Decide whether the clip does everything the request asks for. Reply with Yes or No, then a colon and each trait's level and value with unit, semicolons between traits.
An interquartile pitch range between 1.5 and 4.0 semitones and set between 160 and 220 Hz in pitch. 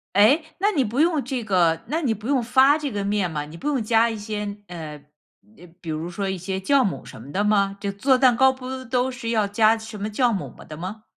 No: average, 4.8 semitones; high, 215 Hz